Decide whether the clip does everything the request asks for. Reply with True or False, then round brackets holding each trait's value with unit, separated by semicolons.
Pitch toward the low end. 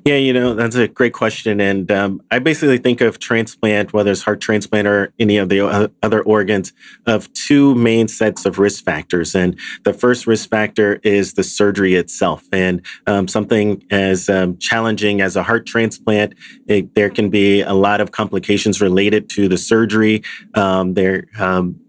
True (105 Hz)